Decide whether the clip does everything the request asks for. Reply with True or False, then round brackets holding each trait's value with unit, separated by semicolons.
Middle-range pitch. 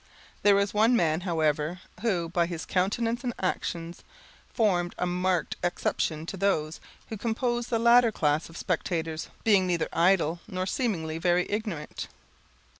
True (180 Hz)